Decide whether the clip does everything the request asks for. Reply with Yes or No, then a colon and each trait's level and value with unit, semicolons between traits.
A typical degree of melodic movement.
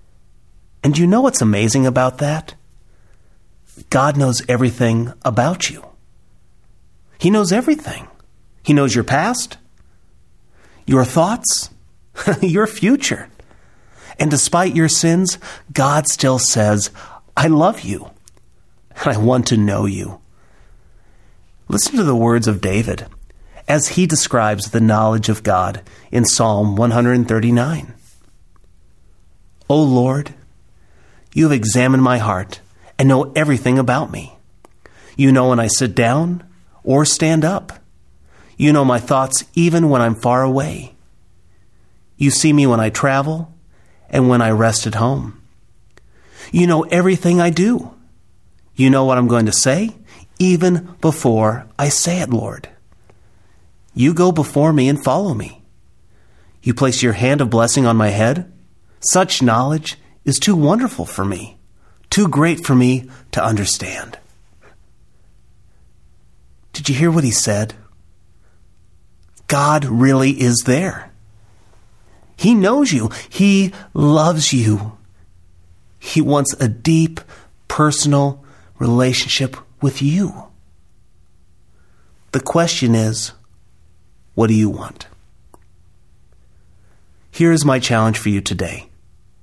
No: wide, 6.0 semitones